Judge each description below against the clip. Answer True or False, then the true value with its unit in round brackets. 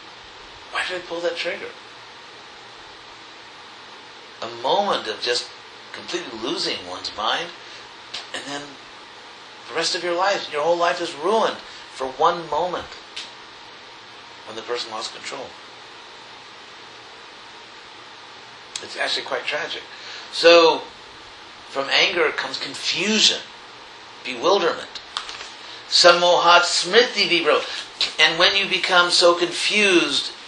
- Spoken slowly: True (105 wpm)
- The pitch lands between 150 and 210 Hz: True (190 Hz)